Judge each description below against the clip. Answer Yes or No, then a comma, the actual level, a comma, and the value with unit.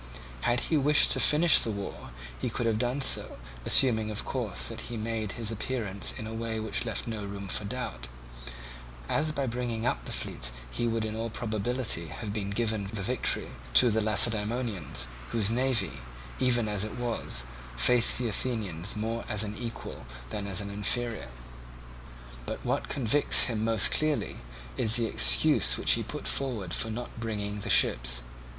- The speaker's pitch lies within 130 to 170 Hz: No, low, 110 Hz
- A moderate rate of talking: Yes, average, 170 wpm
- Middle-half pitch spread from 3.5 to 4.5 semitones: No, average, 2.9 semitones